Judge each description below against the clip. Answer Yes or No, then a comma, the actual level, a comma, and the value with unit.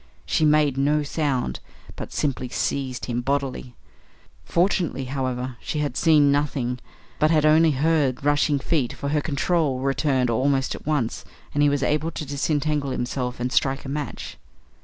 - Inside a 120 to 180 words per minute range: Yes, average, 160 wpm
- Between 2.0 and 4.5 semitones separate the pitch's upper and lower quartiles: Yes, average, 2.7 semitones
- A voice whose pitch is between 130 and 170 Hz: Yes, medium, 140 Hz